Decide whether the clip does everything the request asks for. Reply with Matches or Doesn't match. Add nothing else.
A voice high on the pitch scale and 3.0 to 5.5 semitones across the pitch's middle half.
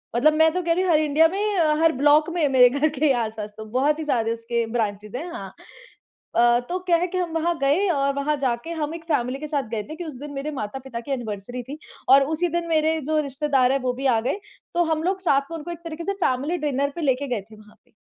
Matches